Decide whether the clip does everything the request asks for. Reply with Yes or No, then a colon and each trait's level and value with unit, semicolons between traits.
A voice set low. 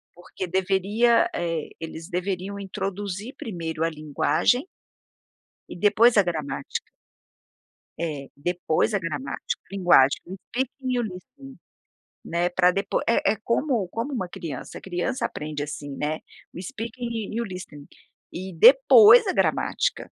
No: medium, 185 Hz